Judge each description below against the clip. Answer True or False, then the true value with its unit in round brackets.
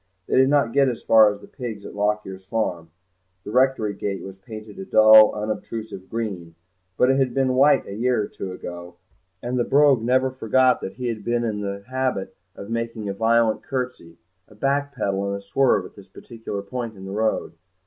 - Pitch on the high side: False (110 Hz)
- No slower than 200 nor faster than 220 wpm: True (205 wpm)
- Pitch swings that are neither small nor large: True (4.2 semitones)